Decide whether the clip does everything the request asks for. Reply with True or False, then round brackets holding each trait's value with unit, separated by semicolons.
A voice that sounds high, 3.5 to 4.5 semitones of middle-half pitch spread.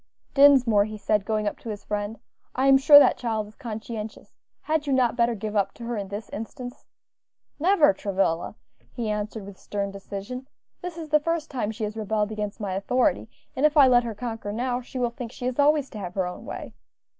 True (225 Hz; 3.9 semitones)